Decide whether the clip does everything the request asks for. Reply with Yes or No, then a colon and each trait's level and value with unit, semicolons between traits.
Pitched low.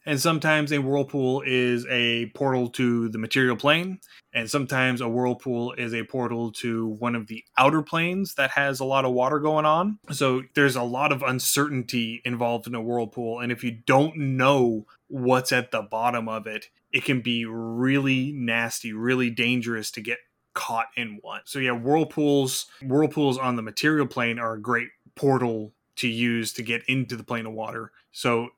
Yes: low, 125 Hz